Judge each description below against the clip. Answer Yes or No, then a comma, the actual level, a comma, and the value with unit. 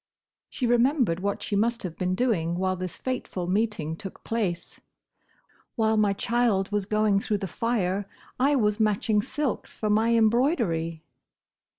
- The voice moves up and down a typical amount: Yes, average, 3.7 semitones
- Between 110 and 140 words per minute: No, average, 150 wpm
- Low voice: No, high, 210 Hz